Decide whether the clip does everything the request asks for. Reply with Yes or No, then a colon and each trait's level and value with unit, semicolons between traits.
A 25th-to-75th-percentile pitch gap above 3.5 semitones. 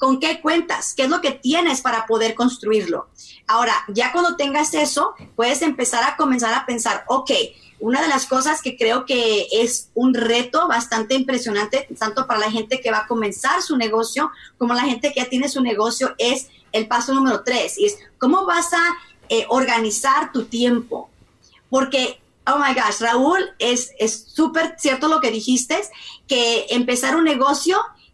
Yes: average, 4.3 semitones